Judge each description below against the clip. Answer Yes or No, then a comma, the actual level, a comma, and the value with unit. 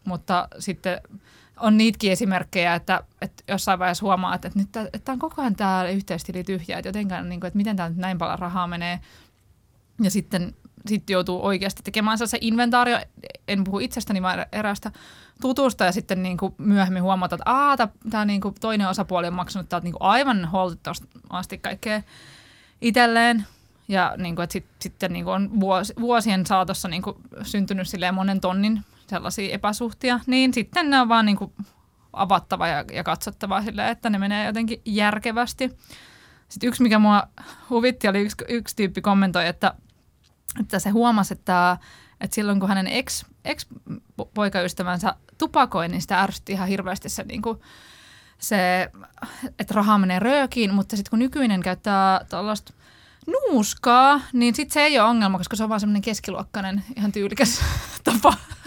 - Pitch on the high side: Yes, high, 200 Hz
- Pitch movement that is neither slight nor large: Yes, average, 3.4 semitones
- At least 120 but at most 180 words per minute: Yes, average, 150 wpm